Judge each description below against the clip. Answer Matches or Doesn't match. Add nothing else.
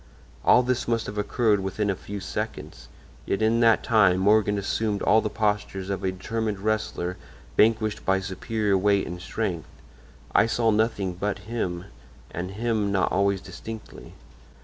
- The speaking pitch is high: Doesn't match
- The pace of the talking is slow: Doesn't match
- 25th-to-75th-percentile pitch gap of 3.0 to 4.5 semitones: Doesn't match